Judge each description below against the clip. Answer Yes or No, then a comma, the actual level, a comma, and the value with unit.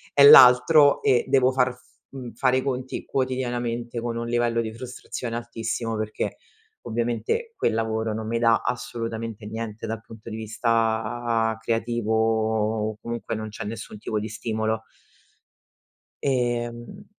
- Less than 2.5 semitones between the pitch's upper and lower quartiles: Yes, narrow, 1.8 semitones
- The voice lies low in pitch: Yes, low, 115 Hz